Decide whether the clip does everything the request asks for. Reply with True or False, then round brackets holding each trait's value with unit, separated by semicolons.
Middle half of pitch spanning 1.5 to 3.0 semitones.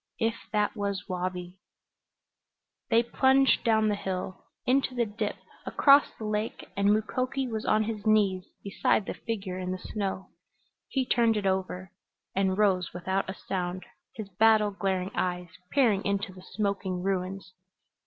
True (2.7 semitones)